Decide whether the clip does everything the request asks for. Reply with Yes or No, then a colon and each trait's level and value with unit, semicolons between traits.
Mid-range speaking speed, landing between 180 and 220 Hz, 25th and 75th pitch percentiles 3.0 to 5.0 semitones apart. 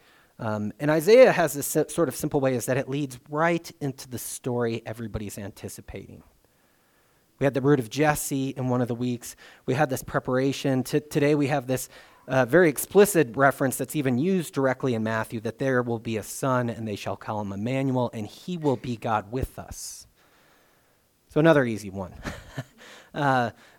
No: average, 185 wpm; low, 130 Hz; average, 4.2 semitones